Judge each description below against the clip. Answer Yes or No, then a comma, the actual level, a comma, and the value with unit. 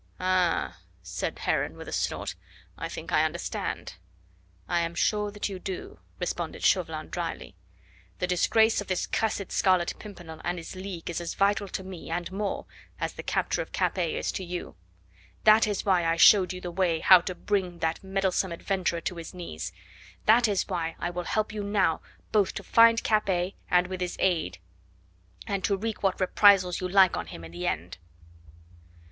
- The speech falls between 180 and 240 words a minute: Yes, average, 185 wpm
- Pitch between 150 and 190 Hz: Yes, medium, 185 Hz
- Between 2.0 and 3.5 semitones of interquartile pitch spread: Yes, narrow, 2.6 semitones